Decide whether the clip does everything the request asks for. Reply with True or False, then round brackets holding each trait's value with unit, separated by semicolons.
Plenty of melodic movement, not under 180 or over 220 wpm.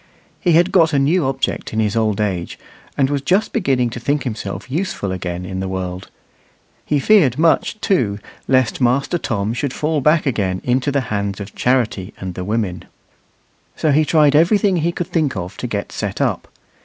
True (7.2 semitones; 190 wpm)